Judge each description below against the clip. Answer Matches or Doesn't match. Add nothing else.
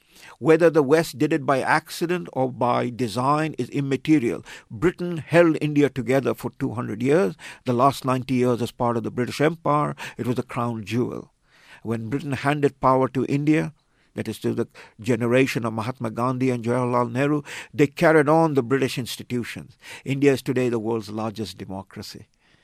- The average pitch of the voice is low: Matches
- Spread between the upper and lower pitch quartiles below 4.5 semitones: Matches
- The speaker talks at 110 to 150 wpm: Doesn't match